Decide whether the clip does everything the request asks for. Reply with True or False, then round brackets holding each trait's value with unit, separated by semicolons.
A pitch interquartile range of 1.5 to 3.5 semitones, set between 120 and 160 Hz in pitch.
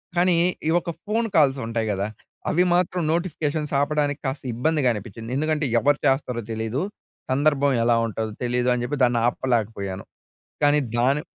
False (4.5 semitones; 135 Hz)